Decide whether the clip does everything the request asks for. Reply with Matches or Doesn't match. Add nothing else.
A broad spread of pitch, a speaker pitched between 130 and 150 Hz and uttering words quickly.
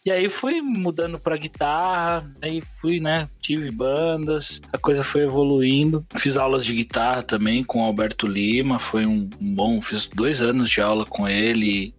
Doesn't match